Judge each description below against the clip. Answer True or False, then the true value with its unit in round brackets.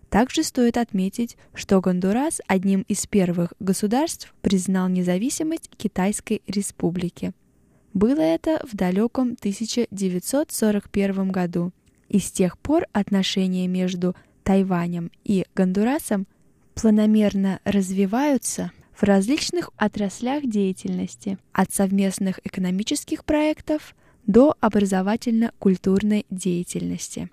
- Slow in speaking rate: True (90 wpm)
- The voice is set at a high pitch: True (200 Hz)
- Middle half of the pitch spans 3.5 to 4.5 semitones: True (3.8 semitones)